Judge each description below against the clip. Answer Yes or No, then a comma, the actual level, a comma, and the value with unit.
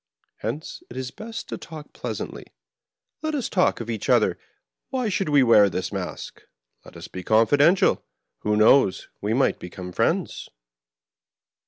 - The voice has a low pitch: Yes, low, 130 Hz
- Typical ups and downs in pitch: No, wide, 8.5 semitones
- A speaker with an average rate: Yes, average, 155 wpm